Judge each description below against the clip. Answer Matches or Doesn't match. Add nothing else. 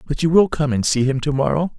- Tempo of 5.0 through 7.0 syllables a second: Matches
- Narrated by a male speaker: Matches